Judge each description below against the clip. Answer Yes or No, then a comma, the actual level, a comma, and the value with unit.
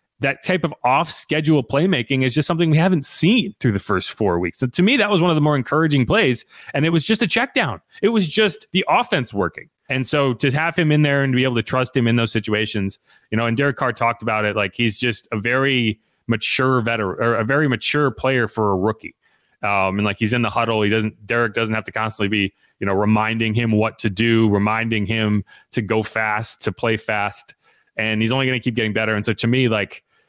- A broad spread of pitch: No, average, 4.4 semitones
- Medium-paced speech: No, fast, 245 wpm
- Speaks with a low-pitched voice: Yes, low, 115 Hz